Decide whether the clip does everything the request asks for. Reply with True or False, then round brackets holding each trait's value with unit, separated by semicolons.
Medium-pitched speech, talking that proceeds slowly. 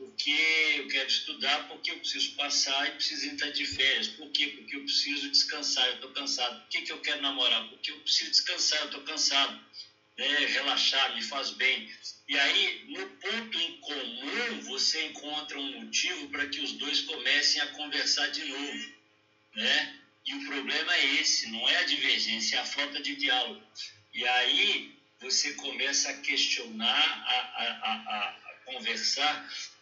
False (150 Hz; 170 wpm)